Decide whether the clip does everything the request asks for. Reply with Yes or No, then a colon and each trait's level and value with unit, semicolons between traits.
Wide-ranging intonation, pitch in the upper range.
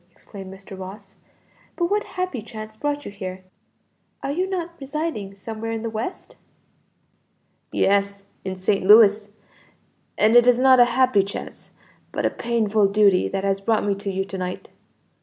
No: average, 4.0 semitones; high, 215 Hz